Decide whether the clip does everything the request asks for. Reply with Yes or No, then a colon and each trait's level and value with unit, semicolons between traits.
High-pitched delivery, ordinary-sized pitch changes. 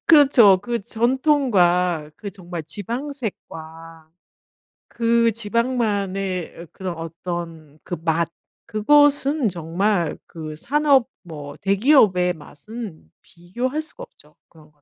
No: high, 195 Hz; wide, 6.4 semitones